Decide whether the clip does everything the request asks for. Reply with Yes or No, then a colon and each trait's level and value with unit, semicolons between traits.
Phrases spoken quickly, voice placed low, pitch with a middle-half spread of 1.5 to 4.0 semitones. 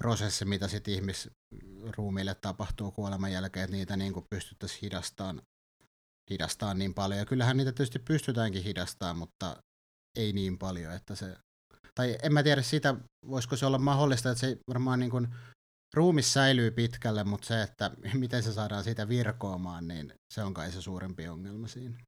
No: fast, 165 wpm; low, 105 Hz; average, 4.6 semitones